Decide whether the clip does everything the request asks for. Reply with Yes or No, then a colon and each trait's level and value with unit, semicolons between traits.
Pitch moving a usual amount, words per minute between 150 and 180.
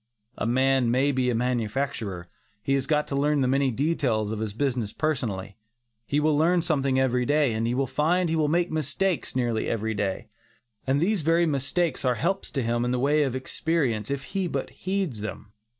No: average, 4.4 semitones; average, 200 wpm